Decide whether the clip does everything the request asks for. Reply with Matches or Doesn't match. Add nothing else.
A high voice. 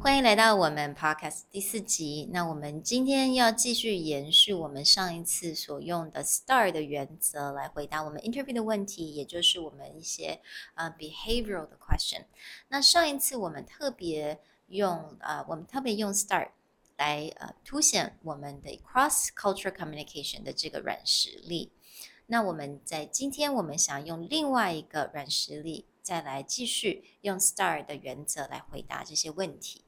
Doesn't match